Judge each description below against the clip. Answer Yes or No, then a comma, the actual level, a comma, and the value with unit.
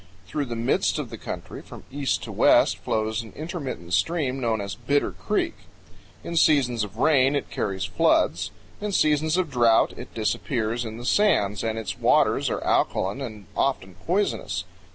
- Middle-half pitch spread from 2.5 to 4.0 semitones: No, average, 5.2 semitones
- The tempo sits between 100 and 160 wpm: No, average, 170 wpm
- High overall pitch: No, low, 120 Hz